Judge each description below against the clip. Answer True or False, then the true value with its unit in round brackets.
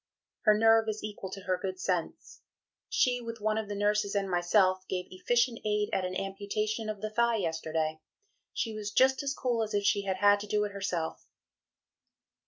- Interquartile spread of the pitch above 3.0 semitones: False (2.5 semitones)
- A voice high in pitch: True (205 Hz)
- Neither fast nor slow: True (190 wpm)